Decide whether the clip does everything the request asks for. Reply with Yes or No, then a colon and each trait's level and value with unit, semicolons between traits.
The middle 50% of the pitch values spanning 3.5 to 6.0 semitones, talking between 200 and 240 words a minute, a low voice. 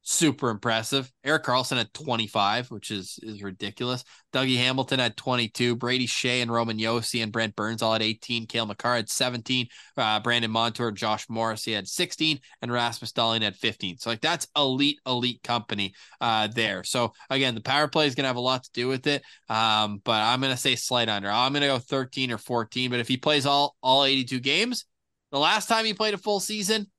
No: average, 3.0 semitones; fast, 205 wpm; low, 125 Hz